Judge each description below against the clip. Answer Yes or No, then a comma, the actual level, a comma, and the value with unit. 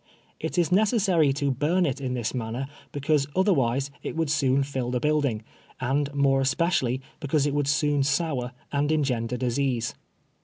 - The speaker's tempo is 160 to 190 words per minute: Yes, average, 165 wpm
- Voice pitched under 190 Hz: Yes, medium, 140 Hz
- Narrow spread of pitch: No, average, 3.0 semitones